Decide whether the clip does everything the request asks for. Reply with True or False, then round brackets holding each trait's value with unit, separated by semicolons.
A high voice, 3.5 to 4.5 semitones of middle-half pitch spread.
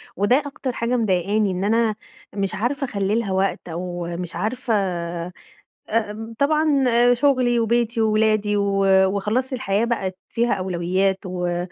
True (215 Hz; 3.9 semitones)